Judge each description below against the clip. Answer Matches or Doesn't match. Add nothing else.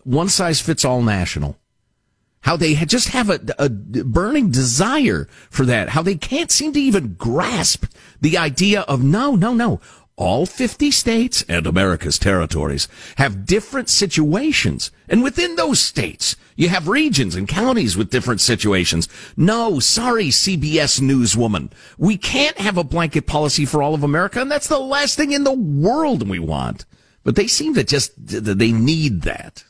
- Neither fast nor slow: Matches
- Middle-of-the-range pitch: Matches